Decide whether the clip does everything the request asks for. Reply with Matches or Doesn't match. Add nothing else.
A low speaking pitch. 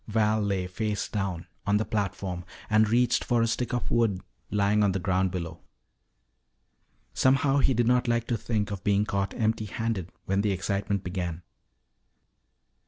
Matches